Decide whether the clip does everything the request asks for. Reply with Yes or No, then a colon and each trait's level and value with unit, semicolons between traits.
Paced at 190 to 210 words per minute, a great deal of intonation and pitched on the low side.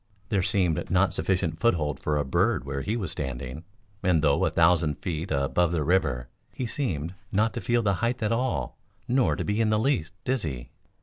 Yes: average, 195 wpm; wide, 6.3 semitones; very low, 90 Hz